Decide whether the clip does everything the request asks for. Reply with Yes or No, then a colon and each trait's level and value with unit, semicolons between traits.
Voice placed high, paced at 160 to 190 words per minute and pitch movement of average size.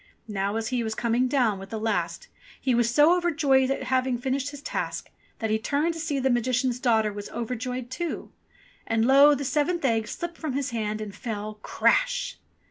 No: very high, 255 Hz; average, 200 wpm; average, 4.3 semitones